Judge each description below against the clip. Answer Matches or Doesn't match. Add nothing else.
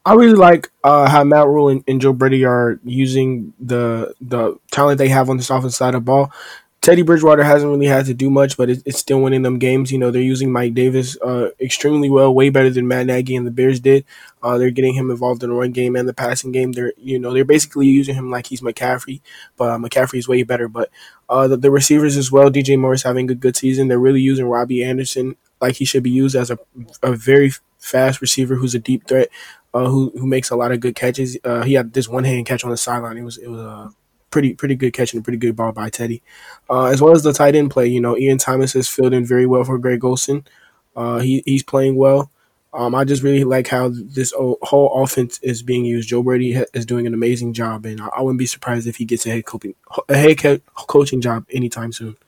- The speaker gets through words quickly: Matches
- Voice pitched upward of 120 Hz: Matches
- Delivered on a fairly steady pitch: Matches